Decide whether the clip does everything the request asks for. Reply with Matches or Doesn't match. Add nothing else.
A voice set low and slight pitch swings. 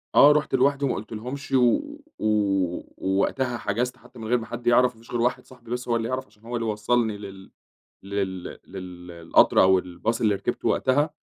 Doesn't match